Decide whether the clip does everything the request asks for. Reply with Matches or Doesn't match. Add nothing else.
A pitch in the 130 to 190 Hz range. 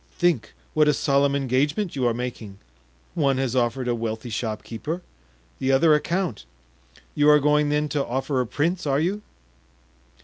Matches